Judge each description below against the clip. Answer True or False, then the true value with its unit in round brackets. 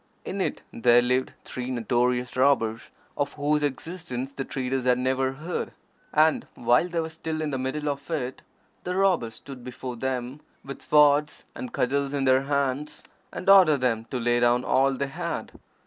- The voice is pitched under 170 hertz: True (135 Hz)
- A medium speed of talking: True (175 wpm)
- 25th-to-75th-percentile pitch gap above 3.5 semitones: False (3.0 semitones)